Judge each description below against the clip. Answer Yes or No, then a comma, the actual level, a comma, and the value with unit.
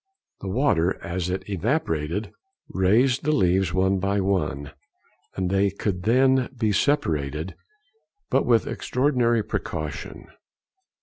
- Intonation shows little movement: No, average, 4.5 semitones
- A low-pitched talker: Yes, very low, 95 Hz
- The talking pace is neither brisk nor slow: No, slow, 110 wpm